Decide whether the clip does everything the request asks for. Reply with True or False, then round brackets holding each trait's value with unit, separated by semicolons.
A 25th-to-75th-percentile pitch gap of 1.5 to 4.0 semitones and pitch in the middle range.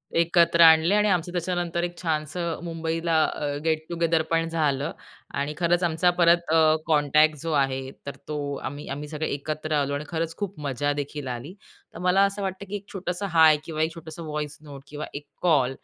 True (2.6 semitones; 160 Hz)